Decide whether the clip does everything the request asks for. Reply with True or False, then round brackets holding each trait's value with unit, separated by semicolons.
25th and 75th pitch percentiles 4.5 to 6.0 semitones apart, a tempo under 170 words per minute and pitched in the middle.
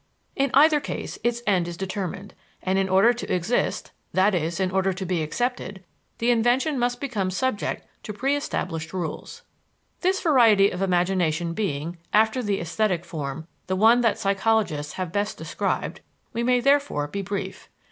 False (5.0 semitones; 155 wpm; 195 Hz)